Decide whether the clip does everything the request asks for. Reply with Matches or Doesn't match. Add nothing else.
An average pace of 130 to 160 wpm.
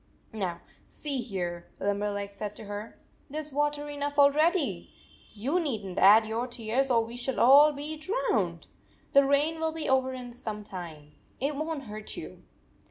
Doesn't match